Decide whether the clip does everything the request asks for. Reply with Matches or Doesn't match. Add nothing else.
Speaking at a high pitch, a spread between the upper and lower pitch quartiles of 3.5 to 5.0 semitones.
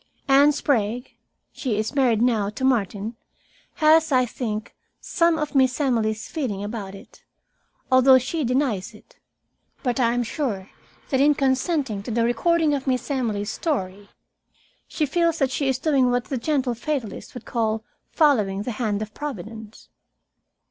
Matches